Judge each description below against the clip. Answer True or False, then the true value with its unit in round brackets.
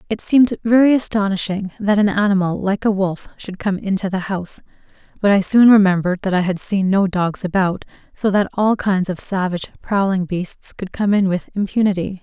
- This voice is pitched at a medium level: False (195 Hz)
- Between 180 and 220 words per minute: True (190 wpm)